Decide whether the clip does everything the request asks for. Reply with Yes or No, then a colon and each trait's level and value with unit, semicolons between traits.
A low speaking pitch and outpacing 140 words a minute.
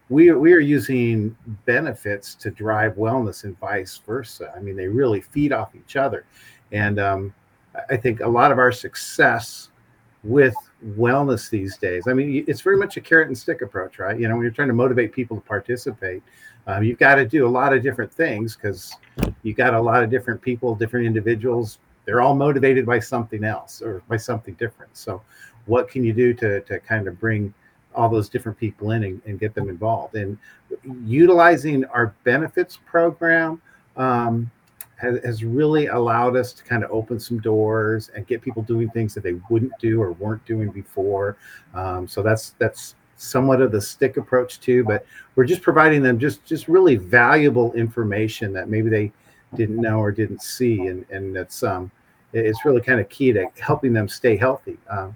Yes: low, 115 Hz; average, 195 wpm